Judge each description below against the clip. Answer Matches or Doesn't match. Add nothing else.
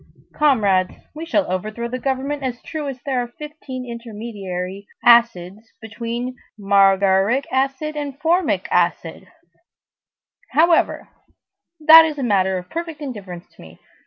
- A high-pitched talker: Matches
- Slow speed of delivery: Matches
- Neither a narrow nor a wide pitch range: Doesn't match